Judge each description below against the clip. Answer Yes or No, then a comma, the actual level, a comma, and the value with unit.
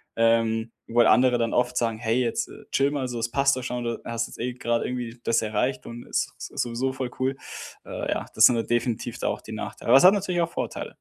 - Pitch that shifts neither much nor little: No, narrow, 2.0 semitones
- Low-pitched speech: Yes, low, 120 Hz